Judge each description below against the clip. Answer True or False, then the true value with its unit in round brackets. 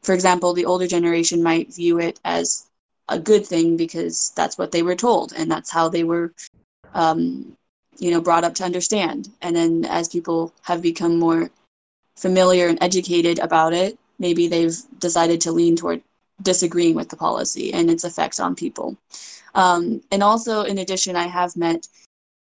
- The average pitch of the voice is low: False (170 Hz)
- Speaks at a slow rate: False (175 wpm)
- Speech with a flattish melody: True (1.4 semitones)